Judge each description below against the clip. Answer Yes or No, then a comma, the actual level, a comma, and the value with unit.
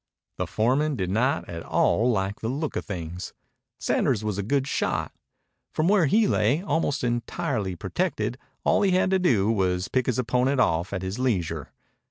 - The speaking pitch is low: Yes, low, 120 Hz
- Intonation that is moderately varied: No, wide, 6.8 semitones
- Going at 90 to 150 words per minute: No, average, 185 wpm